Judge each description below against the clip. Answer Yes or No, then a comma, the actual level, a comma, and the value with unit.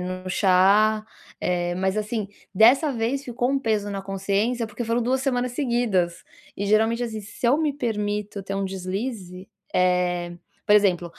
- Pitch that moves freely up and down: No, average, 4.1 semitones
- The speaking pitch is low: No, high, 210 Hz